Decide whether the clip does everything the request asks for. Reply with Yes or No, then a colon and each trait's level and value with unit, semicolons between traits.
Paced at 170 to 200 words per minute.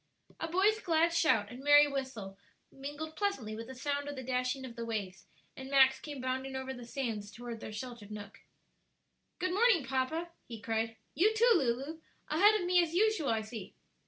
Yes: average, 190 wpm